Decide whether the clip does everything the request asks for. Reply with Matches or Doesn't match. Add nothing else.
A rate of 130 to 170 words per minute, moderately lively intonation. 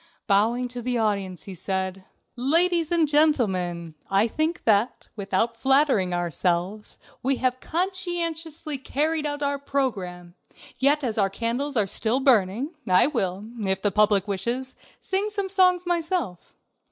Doesn't match